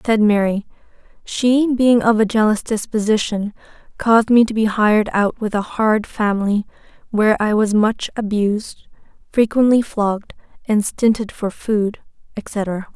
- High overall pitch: Yes, high, 215 Hz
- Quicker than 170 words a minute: No, average, 140 wpm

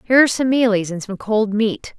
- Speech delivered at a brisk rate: Yes, fast, 240 wpm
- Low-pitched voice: No, high, 220 Hz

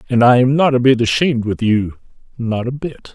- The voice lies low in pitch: Yes, low, 120 Hz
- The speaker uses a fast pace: Yes, fast, 230 wpm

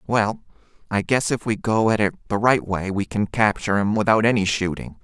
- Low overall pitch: Yes, low, 110 Hz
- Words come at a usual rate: No, fast, 215 wpm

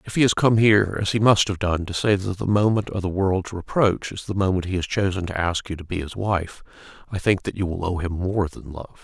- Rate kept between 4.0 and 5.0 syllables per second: No, 5.7 syllables/s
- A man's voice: Yes, male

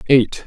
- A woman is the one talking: No, male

